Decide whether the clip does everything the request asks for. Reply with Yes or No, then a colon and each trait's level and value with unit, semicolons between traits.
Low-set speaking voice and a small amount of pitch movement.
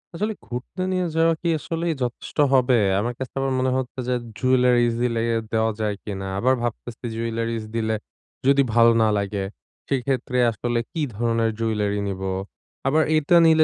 No: low, 120 Hz; average, 3.1 semitones